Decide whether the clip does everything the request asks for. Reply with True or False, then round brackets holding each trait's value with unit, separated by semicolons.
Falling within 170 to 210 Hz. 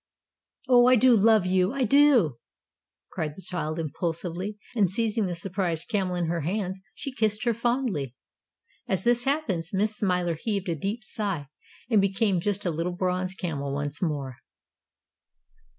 True (190 Hz)